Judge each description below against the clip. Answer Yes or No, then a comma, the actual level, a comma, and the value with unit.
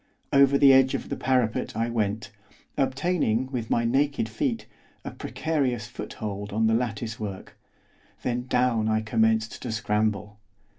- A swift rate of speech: No, average, 140 wpm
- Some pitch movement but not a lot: Yes, average, 3.2 semitones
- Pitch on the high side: No, low, 115 Hz